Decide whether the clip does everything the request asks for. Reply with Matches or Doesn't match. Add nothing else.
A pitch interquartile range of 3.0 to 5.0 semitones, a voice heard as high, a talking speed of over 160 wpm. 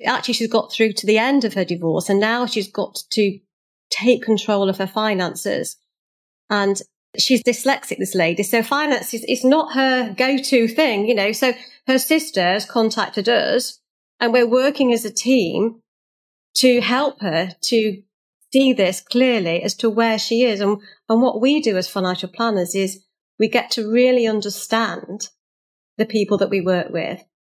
Matches